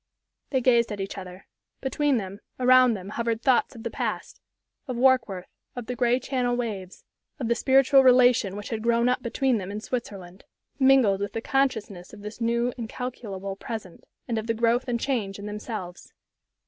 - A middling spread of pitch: Yes, average, 3.7 semitones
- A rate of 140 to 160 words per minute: No, average, 180 wpm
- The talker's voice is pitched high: Yes, high, 235 Hz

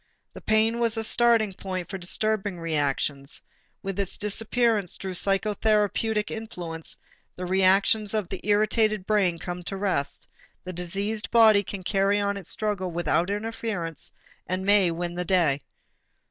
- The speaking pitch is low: No, high, 195 Hz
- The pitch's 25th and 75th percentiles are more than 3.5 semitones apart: No, average, 3.2 semitones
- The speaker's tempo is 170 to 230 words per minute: No, average, 145 wpm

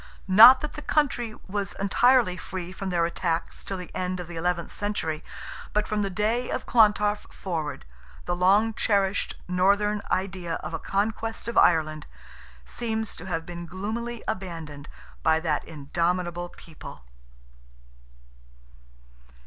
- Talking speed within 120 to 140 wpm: Yes, slow, 135 wpm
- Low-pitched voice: No, medium, 185 Hz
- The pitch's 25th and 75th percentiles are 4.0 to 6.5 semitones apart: No, average, 3.6 semitones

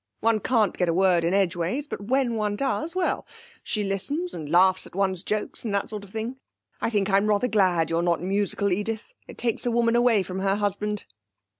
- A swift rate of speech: Yes, fast, 210 wpm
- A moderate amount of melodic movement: Yes, average, 3.4 semitones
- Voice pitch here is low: No, high, 205 Hz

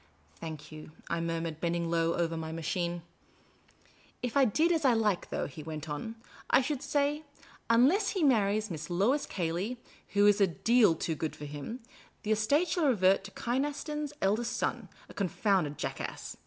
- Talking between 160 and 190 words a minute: Yes, average, 180 wpm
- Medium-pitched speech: No, high, 200 Hz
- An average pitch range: No, wide, 7.3 semitones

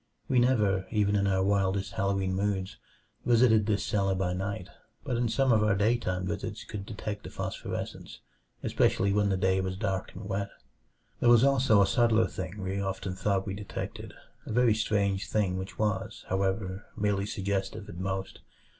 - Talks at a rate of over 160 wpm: Yes, average, 170 wpm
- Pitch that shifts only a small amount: Yes, narrow, 2.0 semitones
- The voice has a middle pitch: No, low, 100 Hz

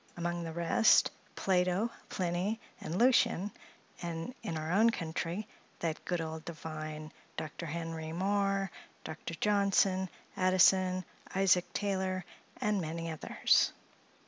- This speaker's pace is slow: Yes, slow, 115 wpm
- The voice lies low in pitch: No, medium, 180 Hz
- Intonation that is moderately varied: Yes, average, 3.1 semitones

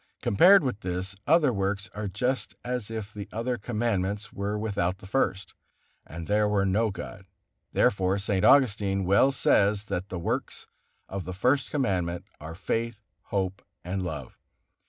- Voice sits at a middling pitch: No, low, 100 Hz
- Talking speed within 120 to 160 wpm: Yes, average, 155 wpm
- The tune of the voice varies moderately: Yes, average, 3.1 semitones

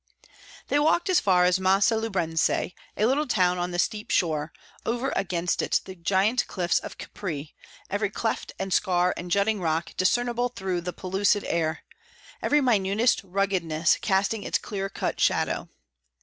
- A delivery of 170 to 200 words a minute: No, average, 155 wpm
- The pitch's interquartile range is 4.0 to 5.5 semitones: No, average, 3.6 semitones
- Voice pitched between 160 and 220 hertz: Yes, high, 190 Hz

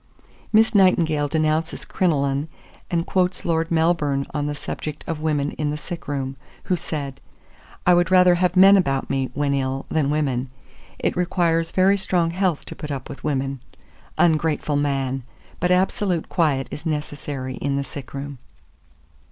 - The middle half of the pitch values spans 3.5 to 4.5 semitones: Yes, average, 3.9 semitones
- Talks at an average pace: Yes, average, 160 wpm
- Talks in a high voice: No, medium, 155 Hz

